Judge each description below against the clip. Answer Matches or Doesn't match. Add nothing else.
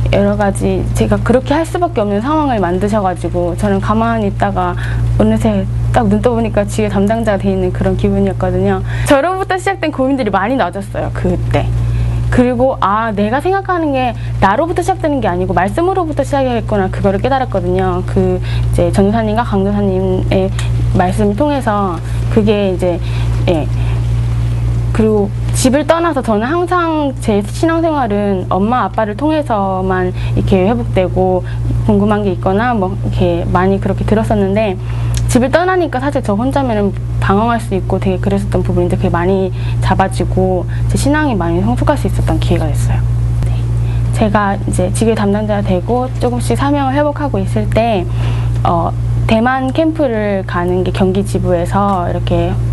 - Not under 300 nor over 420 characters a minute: Matches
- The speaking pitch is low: Matches